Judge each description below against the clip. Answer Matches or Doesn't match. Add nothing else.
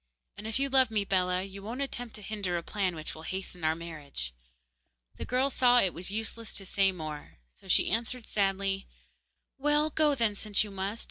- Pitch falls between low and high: Doesn't match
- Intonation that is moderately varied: Matches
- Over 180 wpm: Matches